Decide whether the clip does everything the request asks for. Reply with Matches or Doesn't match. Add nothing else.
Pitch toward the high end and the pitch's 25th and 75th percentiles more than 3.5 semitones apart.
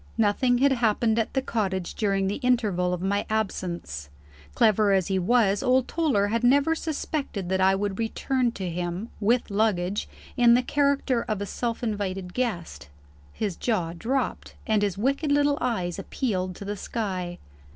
Matches